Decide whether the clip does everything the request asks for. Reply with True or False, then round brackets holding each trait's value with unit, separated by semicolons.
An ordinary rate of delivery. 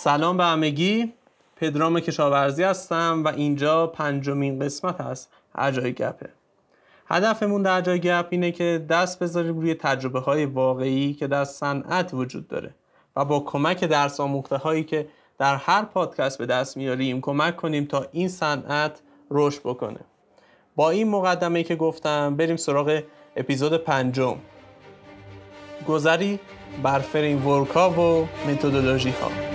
True (135 wpm)